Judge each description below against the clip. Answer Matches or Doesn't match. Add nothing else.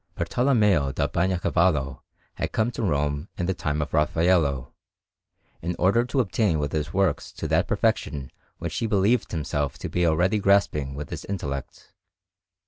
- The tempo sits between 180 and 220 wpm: Doesn't match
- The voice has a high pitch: Doesn't match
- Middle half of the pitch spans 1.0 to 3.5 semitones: Doesn't match